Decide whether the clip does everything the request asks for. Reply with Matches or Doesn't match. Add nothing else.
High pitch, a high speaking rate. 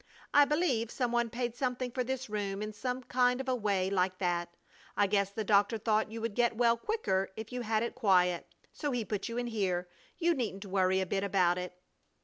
Matches